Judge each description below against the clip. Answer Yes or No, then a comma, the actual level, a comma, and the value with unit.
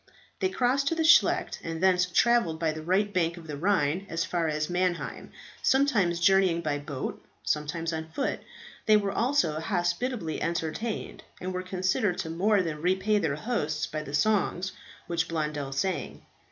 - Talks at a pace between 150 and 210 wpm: Yes, average, 165 wpm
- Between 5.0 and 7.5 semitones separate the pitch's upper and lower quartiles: No, average, 4.1 semitones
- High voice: No, medium, 175 Hz